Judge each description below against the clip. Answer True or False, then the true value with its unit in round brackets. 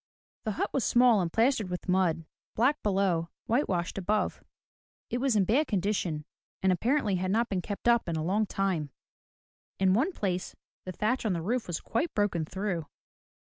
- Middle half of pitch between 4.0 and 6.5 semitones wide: True (4.3 semitones)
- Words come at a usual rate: True (180 wpm)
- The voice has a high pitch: True (195 Hz)